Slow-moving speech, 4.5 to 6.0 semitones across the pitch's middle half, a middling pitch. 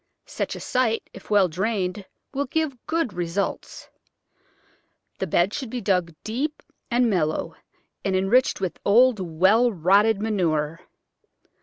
No: slow, 130 wpm; average, 5.0 semitones; high, 200 Hz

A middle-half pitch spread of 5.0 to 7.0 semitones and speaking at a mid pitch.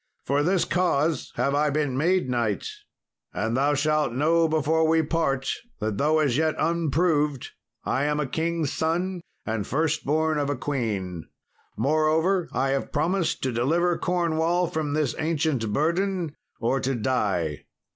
No: average, 3.5 semitones; medium, 150 Hz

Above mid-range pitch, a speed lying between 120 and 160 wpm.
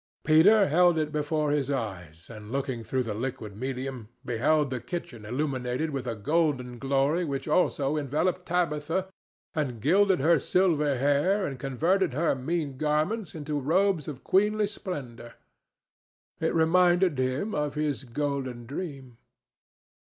No: medium, 145 Hz; average, 140 wpm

